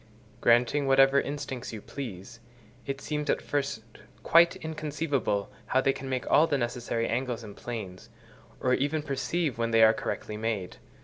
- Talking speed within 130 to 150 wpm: No, average, 160 wpm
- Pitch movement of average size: Yes, average, 3.8 semitones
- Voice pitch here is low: Yes, low, 130 Hz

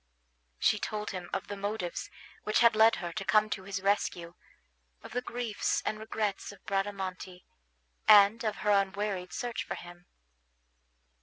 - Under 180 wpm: Yes, average, 155 wpm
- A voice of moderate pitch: No, high, 200 Hz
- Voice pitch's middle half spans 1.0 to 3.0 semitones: Yes, narrow, 2.4 semitones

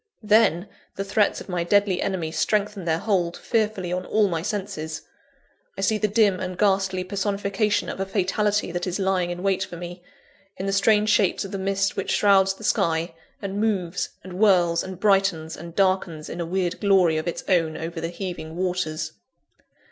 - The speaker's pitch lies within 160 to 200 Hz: Yes, high, 190 Hz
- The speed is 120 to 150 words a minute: No, average, 185 wpm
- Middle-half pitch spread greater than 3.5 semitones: No, narrow, 2.6 semitones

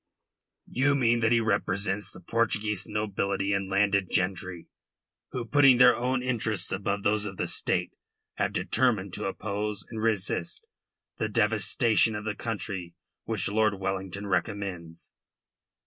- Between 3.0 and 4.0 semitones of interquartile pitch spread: No, narrow, 2.6 semitones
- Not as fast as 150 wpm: Yes, slow, 135 wpm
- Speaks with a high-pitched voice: No, low, 105 Hz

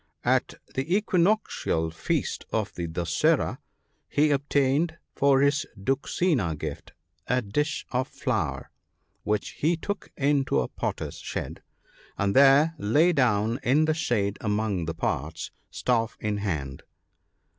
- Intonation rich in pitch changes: Yes, wide, 6.4 semitones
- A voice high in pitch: No, low, 130 Hz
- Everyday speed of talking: No, slow, 125 wpm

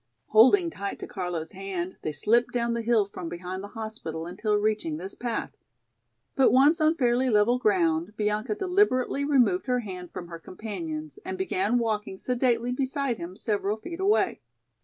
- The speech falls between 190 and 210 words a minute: No, average, 165 wpm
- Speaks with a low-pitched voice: No, high, 220 Hz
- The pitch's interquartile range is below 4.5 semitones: No, average, 5.2 semitones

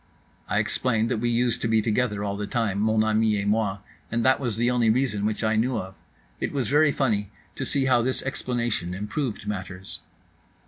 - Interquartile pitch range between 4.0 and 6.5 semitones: No, average, 3.1 semitones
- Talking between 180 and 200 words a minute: Yes, average, 190 wpm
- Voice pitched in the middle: No, low, 110 Hz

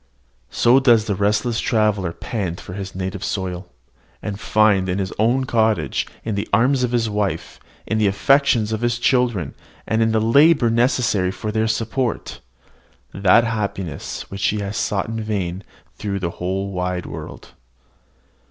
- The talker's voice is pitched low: Yes, low, 105 Hz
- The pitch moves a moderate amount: Yes, average, 3.0 semitones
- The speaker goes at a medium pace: Yes, average, 155 wpm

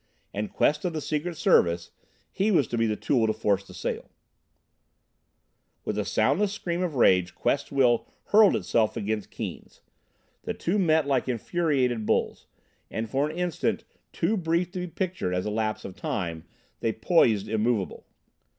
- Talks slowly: No, average, 165 wpm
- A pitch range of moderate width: No, wide, 8.1 semitones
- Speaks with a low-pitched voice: Yes, low, 130 Hz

